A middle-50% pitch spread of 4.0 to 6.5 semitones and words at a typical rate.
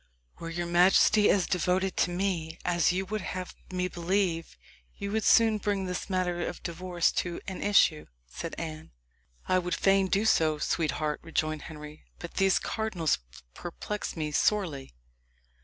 No: average, 2.8 semitones; average, 155 wpm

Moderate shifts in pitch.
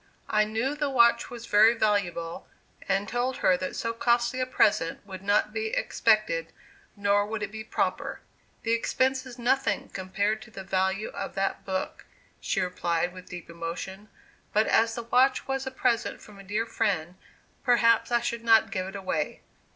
Yes: average, 3.6 semitones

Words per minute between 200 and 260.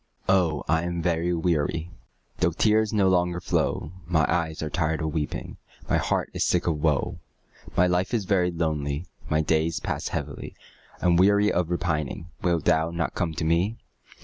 No: average, 175 wpm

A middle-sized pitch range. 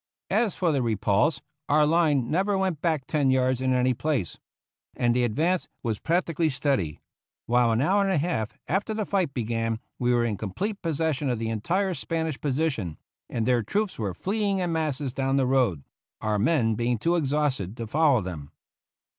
No: wide, 6.2 semitones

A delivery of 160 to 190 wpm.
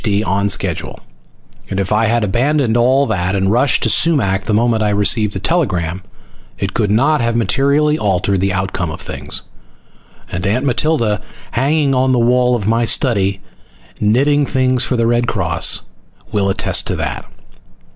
Yes: average, 165 wpm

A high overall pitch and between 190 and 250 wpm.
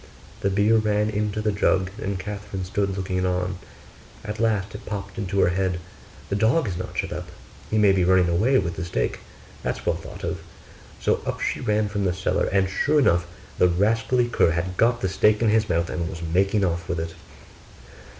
No: low, 100 Hz; fast, 205 wpm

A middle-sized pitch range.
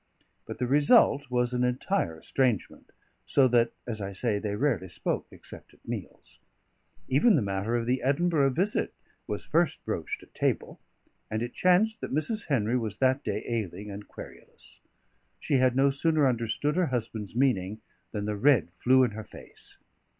Yes: average, 4.7 semitones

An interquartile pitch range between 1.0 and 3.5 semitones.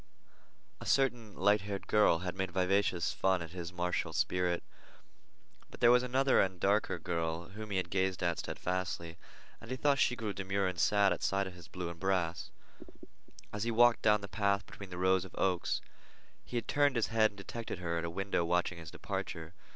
Yes: average, 3.1 semitones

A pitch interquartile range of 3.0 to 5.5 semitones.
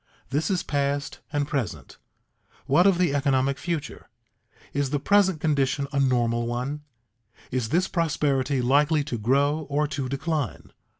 No: narrow, 2.5 semitones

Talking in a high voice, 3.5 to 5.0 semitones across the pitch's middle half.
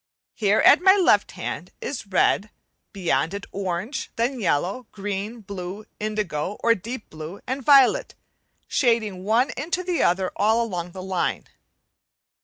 Yes: high, 210 Hz; average, 4.5 semitones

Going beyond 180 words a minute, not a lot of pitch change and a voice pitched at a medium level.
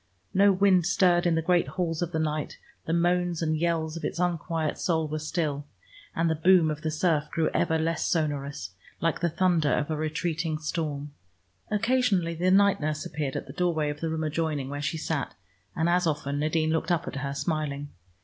Yes: average, 200 wpm; narrow, 2.3 semitones; medium, 160 Hz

